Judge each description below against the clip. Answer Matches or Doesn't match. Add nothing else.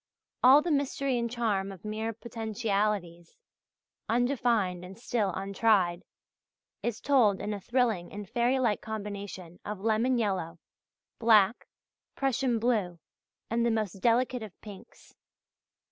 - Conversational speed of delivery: Doesn't match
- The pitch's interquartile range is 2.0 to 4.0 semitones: Matches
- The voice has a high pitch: Matches